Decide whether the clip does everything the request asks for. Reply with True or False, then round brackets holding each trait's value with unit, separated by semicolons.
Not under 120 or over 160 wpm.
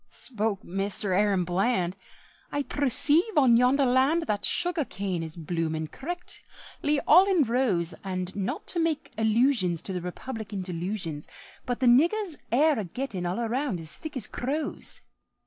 True (145 wpm)